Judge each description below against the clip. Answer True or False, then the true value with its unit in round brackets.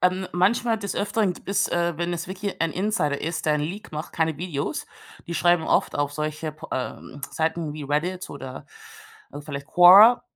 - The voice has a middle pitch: True (170 Hz)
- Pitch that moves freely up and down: False (3.6 semitones)